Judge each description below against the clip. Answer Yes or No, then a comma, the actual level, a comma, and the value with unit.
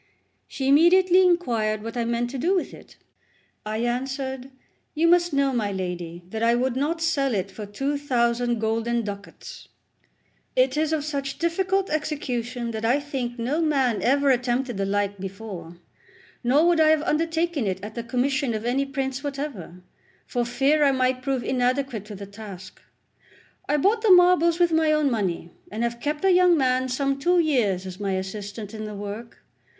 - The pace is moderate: Yes, average, 180 wpm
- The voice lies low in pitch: No, very high, 255 Hz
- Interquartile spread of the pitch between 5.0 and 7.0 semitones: Yes, wide, 5.4 semitones